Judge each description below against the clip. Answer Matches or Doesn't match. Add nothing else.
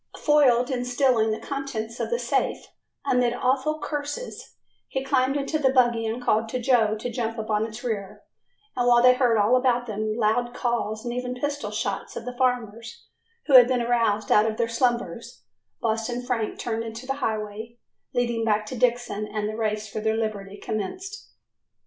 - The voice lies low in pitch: Doesn't match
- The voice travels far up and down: Doesn't match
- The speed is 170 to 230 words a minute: Matches